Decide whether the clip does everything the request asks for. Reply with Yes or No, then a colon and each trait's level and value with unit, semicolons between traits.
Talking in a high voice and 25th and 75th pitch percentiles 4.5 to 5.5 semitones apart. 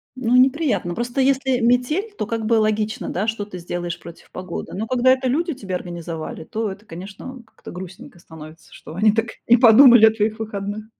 Yes: high, 220 Hz; average, 5.1 semitones